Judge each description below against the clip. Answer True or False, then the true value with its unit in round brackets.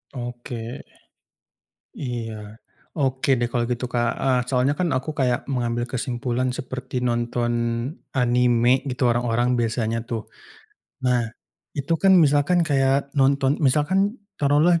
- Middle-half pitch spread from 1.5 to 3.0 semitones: True (2.5 semitones)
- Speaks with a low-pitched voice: True (125 Hz)